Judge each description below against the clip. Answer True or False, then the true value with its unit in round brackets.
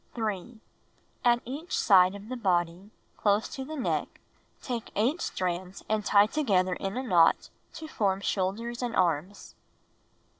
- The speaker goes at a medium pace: True (145 wpm)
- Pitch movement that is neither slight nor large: True (4.5 semitones)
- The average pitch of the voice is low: False (205 Hz)